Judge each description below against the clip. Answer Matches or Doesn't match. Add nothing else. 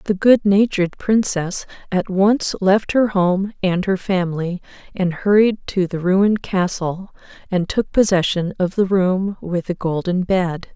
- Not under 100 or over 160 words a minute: Matches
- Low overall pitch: Doesn't match